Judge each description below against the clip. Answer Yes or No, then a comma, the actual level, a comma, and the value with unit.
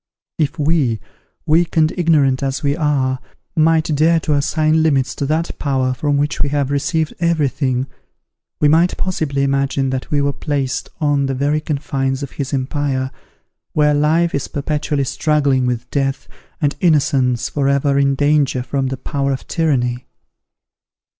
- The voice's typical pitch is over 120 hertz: Yes, medium, 140 Hz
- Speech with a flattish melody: Yes, narrow, 2.2 semitones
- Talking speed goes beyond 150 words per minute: Yes, average, 160 wpm